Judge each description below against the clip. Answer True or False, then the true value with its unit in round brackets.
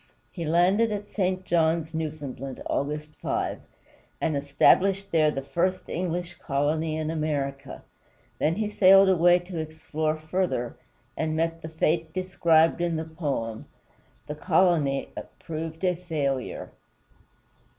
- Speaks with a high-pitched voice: False (160 Hz)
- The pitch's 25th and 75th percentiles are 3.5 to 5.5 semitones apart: False (2.6 semitones)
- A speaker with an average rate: False (130 wpm)